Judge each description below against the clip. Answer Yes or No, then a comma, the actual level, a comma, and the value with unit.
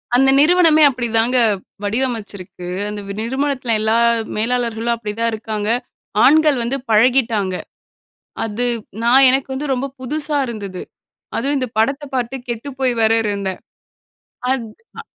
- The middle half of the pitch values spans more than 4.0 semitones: No, average, 3.5 semitones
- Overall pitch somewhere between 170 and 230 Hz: No, high, 240 Hz